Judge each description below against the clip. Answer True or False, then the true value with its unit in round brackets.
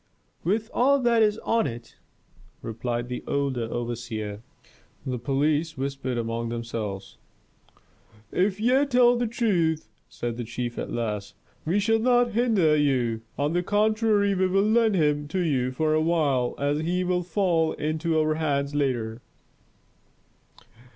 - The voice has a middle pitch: True (155 Hz)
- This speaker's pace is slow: False (145 wpm)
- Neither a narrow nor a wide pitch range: False (8.6 semitones)